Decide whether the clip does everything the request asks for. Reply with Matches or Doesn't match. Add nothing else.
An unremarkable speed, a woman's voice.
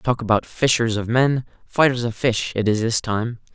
Doesn't match